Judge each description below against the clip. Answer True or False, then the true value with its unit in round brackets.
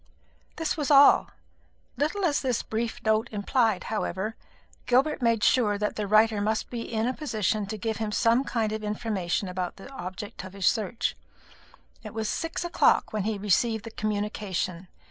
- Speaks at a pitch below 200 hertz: False (220 Hz)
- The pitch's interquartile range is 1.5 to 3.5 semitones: True (2.5 semitones)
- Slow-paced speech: False (170 wpm)